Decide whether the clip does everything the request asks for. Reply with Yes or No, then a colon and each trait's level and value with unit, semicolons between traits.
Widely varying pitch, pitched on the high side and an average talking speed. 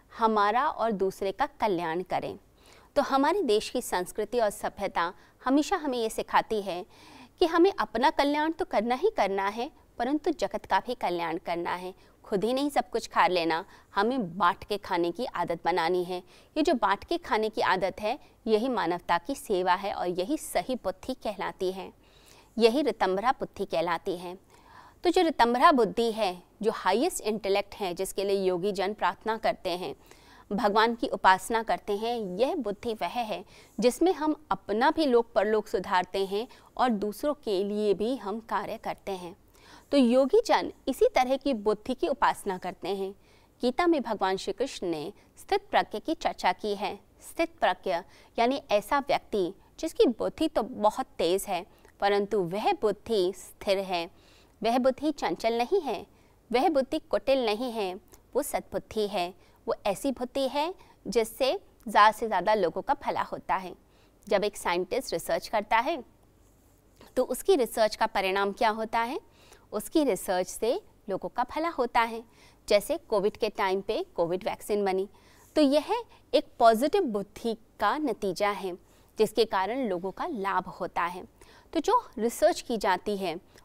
Yes: wide, 6.0 semitones; high, 220 Hz; average, 165 wpm